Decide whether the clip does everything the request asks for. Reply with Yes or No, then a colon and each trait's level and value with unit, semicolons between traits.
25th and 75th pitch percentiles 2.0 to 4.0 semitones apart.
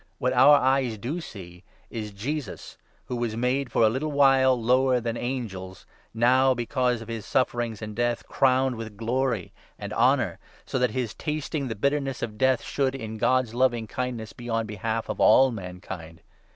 Yes: average, 3.0 semitones